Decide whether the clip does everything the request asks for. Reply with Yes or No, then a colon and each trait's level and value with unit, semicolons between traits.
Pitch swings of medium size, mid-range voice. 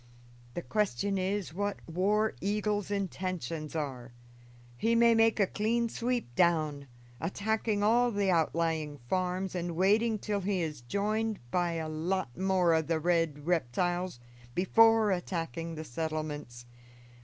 Yes: average, 4.5 semitones; medium, 180 Hz